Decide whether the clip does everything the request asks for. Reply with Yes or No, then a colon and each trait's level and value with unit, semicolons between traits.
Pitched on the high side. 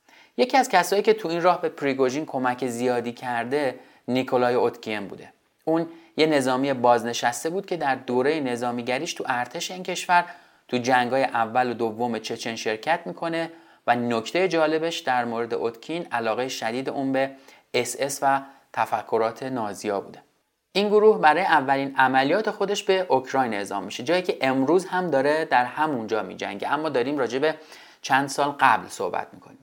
No: low, 135 Hz